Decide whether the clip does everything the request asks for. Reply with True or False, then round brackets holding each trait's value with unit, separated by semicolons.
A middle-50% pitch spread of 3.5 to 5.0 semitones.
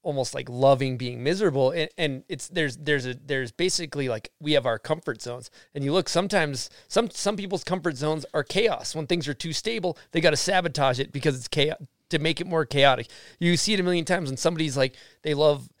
True (4.0 semitones)